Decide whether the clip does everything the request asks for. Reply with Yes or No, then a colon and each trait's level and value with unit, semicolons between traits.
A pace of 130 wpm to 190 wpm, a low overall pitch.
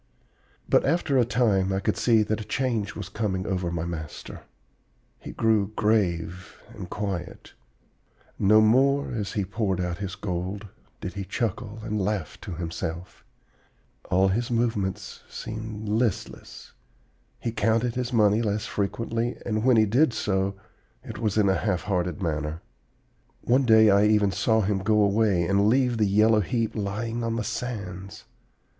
Yes: average, 155 wpm; low, 105 Hz